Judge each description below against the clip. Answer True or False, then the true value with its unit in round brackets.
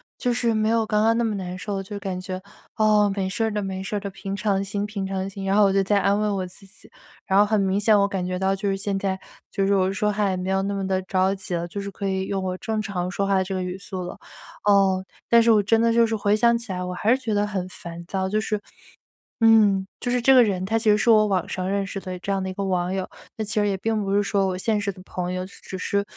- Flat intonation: True (1.9 semitones)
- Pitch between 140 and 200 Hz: True (195 Hz)